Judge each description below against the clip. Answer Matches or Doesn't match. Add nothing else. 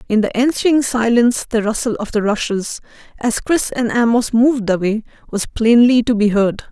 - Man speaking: Doesn't match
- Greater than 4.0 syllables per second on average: Matches